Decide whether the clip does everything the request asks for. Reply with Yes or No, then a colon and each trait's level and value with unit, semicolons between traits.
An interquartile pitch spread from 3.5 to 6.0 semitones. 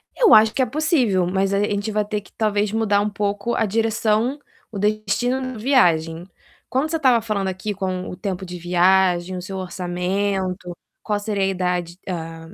No: average, 3.1 semitones